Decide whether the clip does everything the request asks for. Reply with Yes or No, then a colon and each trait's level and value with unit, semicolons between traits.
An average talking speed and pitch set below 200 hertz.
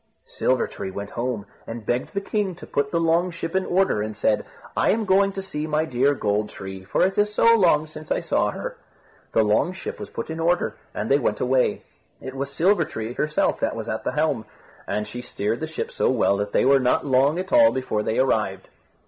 No: fast, 230 wpm; medium, 140 Hz